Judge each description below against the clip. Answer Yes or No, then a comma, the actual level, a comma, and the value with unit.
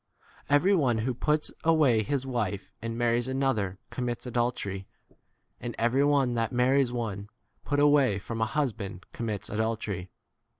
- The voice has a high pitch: No, low, 120 Hz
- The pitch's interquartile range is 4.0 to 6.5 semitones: No, average, 3.6 semitones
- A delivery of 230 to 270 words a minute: No, average, 145 wpm